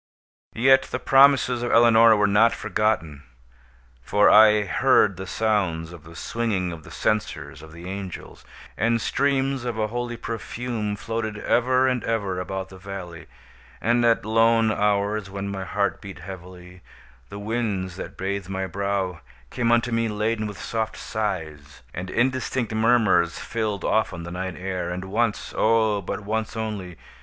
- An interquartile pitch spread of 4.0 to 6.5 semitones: No, average, 3.4 semitones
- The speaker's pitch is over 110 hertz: No, low, 105 Hz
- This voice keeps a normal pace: Yes, average, 155 wpm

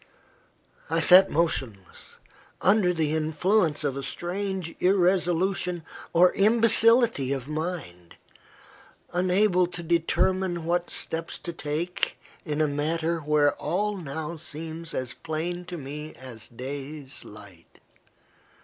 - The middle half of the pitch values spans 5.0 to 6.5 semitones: No, average, 3.5 semitones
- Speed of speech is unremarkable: No, slow, 115 wpm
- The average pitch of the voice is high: No, medium, 165 Hz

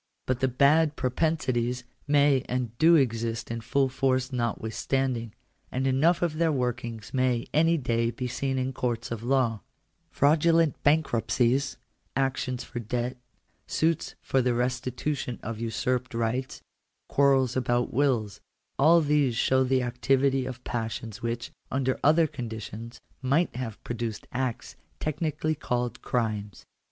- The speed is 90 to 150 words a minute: Yes, slow, 135 wpm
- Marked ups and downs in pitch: No, average, 2.8 semitones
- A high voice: No, low, 130 Hz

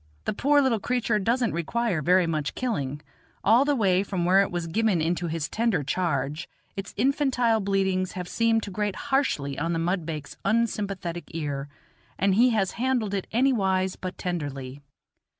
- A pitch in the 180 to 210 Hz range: Yes, high, 190 Hz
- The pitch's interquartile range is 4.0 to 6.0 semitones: Yes, wide, 5.4 semitones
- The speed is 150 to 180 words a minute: Yes, average, 165 wpm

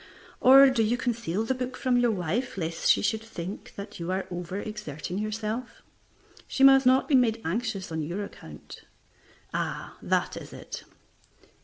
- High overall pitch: Yes, high, 215 Hz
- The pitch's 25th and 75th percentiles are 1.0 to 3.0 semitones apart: No, average, 5.1 semitones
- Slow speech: No, average, 165 wpm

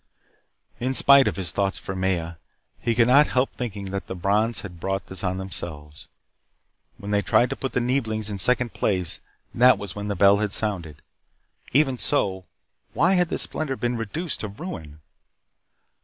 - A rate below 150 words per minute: No, average, 175 wpm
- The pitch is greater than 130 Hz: No, low, 105 Hz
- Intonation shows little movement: No, average, 4.9 semitones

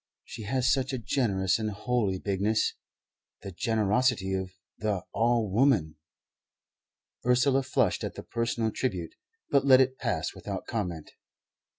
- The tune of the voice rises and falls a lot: No, average, 4.8 semitones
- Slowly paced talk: Yes, slow, 130 wpm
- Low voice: Yes, low, 110 Hz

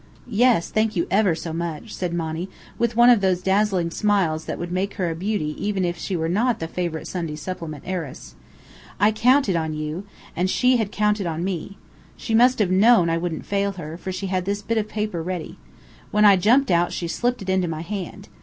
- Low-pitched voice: No, medium, 185 Hz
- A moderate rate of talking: No, fast, 215 wpm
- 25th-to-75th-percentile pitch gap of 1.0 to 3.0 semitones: No, average, 3.8 semitones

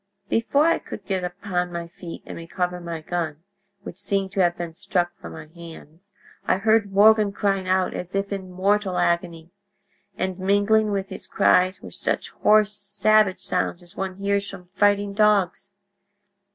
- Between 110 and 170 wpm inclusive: Yes, average, 165 wpm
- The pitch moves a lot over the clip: No, narrow, 2.5 semitones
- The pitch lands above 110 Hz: Yes, high, 190 Hz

